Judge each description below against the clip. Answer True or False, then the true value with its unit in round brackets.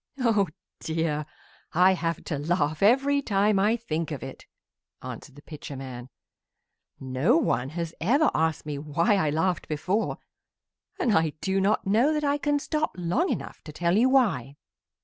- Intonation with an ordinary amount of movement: False (7.0 semitones)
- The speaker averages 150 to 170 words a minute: True (165 wpm)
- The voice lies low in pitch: False (175 Hz)